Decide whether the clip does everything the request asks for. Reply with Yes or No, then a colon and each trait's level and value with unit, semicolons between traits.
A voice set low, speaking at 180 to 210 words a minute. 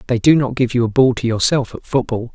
No: low, 125 Hz; fast, 280 wpm